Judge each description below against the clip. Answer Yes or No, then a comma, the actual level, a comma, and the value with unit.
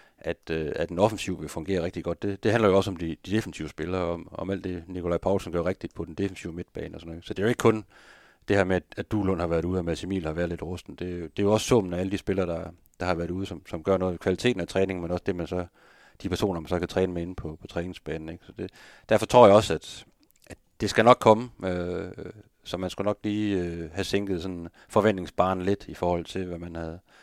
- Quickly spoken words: Yes, fast, 275 wpm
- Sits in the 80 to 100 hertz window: Yes, very low, 90 Hz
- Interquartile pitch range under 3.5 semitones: Yes, narrow, 2.5 semitones